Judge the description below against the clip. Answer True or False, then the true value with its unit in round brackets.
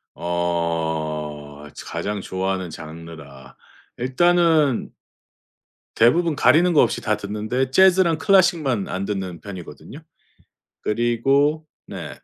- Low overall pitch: True (105 Hz)